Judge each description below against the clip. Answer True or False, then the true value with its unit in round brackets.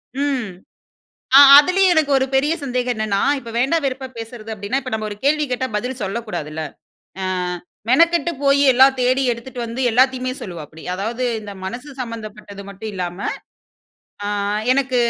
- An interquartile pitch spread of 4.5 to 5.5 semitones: False (4.0 semitones)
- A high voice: True (250 Hz)